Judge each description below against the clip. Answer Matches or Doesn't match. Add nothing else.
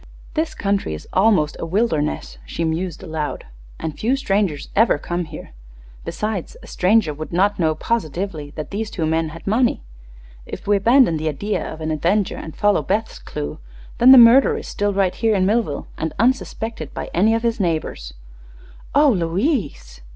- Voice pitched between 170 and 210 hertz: Matches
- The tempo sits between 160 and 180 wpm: Matches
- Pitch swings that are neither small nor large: Doesn't match